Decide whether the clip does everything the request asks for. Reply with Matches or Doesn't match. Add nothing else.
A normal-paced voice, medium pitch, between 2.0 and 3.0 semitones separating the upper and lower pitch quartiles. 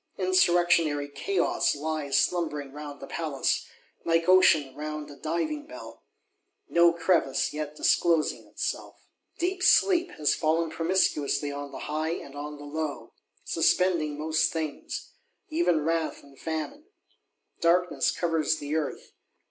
Doesn't match